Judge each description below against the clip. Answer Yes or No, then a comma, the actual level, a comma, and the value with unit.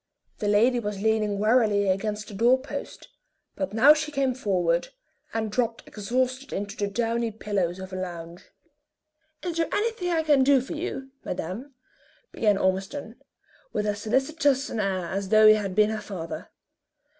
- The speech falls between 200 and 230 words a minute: No, average, 165 wpm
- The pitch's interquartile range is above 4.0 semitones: Yes, average, 4.7 semitones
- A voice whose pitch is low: No, high, 215 Hz